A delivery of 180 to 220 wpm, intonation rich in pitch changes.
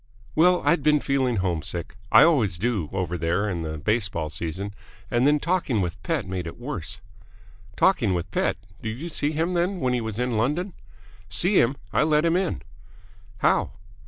Yes: average, 185 wpm; wide, 8.5 semitones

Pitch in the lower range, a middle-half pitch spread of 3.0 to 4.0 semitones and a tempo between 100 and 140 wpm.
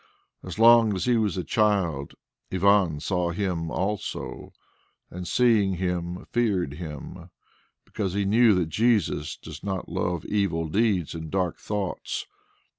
Yes: very low, 95 Hz; average, 3.4 semitones; slow, 135 wpm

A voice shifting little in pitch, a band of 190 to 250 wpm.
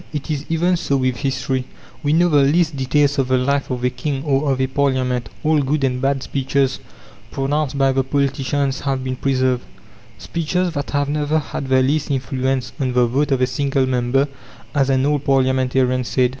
Yes: narrow, 1.8 semitones; average, 195 wpm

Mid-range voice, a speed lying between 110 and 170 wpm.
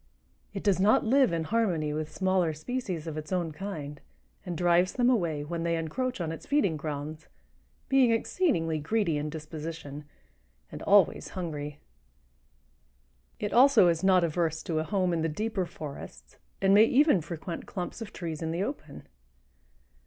Yes: medium, 170 Hz; average, 160 wpm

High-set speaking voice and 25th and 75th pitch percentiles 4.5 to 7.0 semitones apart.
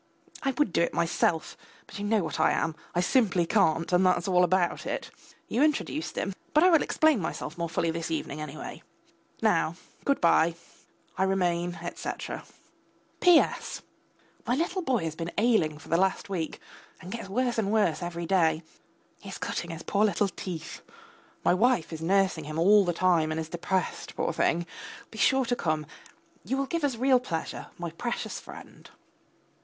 No: medium, 180 Hz; wide, 5.4 semitones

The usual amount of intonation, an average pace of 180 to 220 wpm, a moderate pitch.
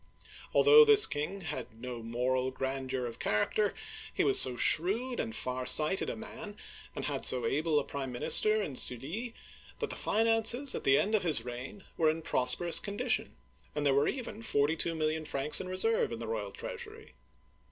No: wide, 8.8 semitones; average, 185 wpm; medium, 155 Hz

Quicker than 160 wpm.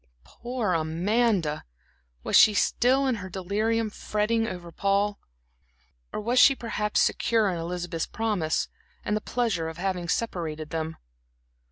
No: slow, 135 wpm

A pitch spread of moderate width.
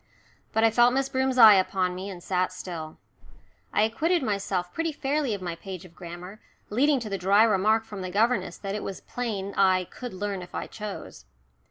Yes: average, 3.9 semitones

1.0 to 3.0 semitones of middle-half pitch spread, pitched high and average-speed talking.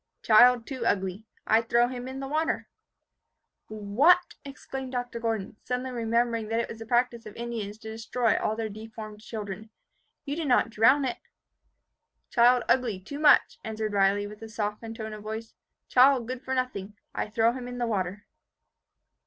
Yes: narrow, 2.6 semitones; high, 230 Hz; average, 175 wpm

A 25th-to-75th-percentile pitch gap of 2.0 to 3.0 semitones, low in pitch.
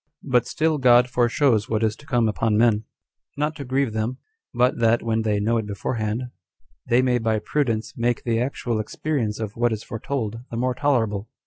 Yes: narrow, 2.5 semitones; low, 115 Hz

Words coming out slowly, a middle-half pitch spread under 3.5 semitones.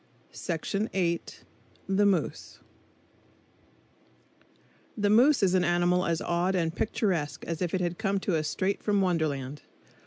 Yes: slow, 125 wpm; average, 2.8 semitones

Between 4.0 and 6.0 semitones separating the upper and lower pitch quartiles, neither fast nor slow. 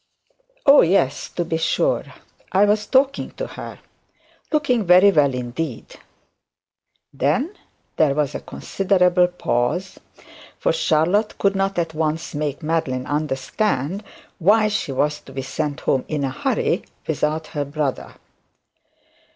No: wide, 5.6 semitones; slow, 130 wpm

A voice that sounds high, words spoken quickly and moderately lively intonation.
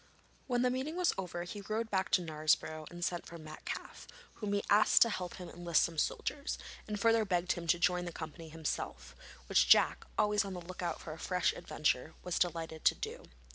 No: medium, 175 Hz; fast, 210 wpm; average, 4.1 semitones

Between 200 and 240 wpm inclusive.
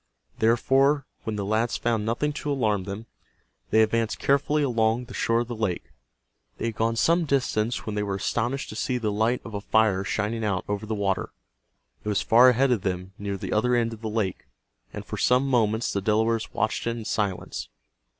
Yes: fast, 205 wpm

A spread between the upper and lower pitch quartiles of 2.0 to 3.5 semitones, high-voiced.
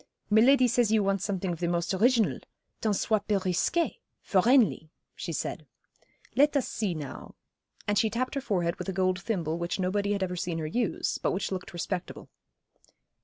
No: average, 3.9 semitones; high, 195 Hz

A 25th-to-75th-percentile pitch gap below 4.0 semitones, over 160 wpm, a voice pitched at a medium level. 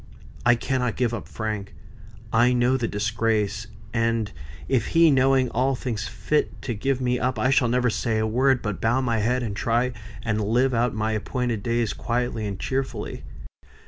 No: narrow, 2.6 semitones; average, 175 wpm; low, 120 Hz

